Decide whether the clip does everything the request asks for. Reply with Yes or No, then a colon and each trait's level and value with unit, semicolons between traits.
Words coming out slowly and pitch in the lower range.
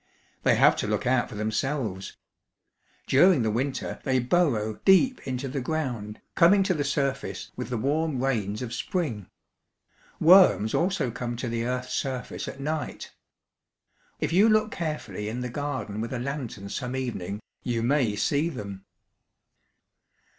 No: average, 150 wpm; low, 130 Hz